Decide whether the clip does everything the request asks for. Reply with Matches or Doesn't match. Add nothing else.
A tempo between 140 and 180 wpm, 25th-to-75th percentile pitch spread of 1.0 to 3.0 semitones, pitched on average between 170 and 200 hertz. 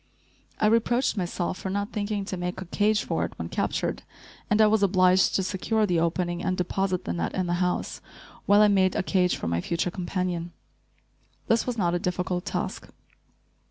Doesn't match